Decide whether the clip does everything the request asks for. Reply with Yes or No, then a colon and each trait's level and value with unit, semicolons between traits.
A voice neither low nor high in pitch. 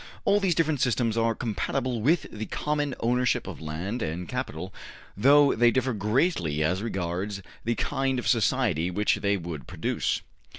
No: low, 115 Hz